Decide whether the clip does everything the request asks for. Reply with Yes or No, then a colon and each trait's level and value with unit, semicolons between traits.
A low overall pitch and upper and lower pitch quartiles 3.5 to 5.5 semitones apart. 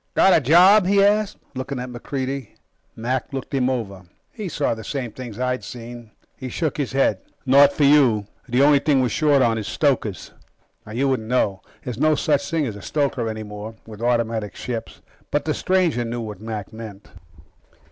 Yes: low, 125 Hz; average, 4.2 semitones